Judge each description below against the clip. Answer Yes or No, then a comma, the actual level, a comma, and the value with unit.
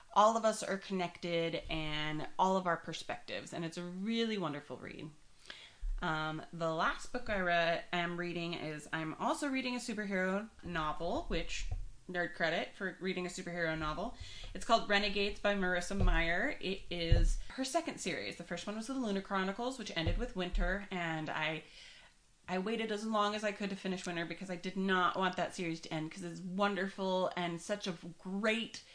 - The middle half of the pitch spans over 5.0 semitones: No, average, 3.5 semitones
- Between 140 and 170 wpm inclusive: No, average, 185 wpm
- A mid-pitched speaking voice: Yes, medium, 180 Hz